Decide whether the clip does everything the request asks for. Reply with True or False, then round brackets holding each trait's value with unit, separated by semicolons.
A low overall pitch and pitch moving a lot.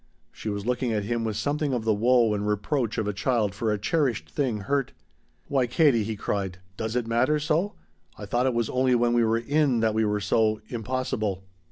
False (115 Hz; 3.4 semitones)